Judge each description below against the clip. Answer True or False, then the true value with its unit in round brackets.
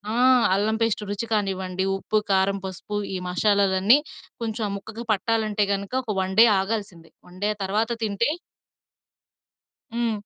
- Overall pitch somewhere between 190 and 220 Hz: True (205 Hz)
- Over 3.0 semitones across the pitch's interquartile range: False (2.6 semitones)